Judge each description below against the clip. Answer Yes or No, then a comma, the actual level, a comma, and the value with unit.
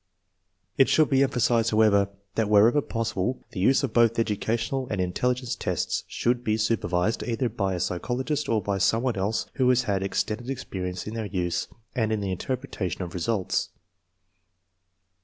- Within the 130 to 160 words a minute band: No, average, 175 wpm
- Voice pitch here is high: No, low, 110 Hz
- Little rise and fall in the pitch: No, average, 4.0 semitones